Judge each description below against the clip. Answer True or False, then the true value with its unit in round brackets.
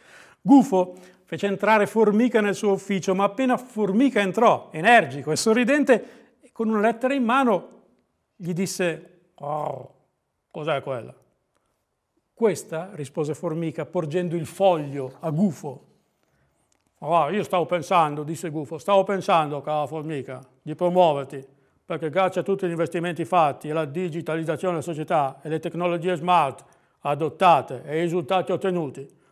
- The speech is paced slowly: False (135 wpm)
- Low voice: False (175 Hz)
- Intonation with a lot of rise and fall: False (4.1 semitones)